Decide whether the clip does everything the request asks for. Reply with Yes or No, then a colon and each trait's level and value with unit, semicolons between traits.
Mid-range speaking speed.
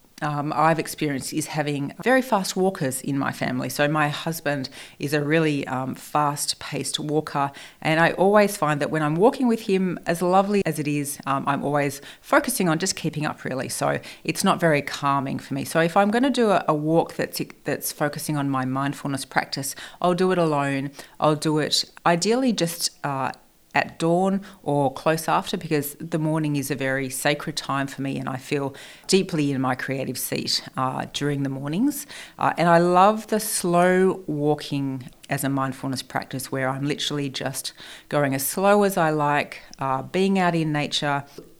Yes: average, 190 wpm